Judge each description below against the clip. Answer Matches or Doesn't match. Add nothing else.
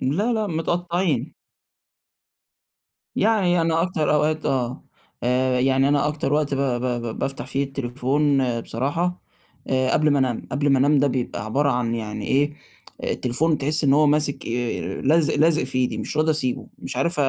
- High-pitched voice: Doesn't match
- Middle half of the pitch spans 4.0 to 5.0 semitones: Doesn't match